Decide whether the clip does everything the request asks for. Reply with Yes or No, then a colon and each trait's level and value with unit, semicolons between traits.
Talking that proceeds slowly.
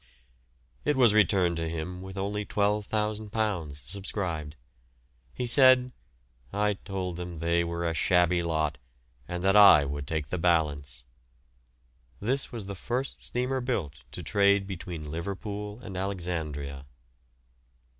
Yes: slow, 125 wpm